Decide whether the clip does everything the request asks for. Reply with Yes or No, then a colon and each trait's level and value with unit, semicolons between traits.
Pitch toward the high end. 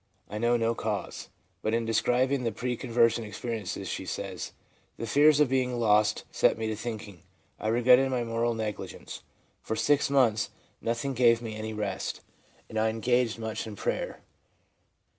No: low, 115 Hz